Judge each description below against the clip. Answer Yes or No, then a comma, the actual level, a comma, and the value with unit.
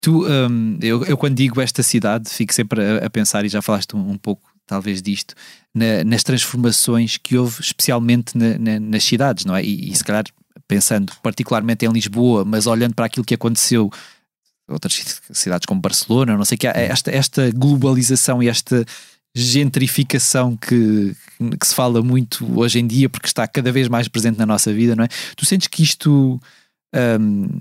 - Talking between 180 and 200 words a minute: Yes, fast, 185 wpm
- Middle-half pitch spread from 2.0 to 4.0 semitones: Yes, average, 2.8 semitones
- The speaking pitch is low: Yes, low, 120 Hz